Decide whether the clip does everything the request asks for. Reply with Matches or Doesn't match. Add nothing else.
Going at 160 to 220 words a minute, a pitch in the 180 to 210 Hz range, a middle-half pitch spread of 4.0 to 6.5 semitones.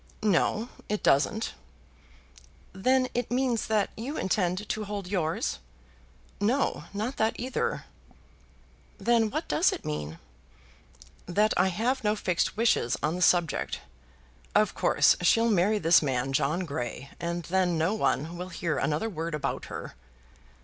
Doesn't match